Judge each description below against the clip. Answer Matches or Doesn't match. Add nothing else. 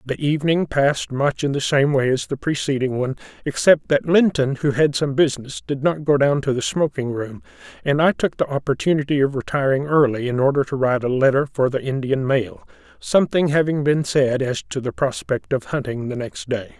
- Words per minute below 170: Doesn't match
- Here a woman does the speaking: Doesn't match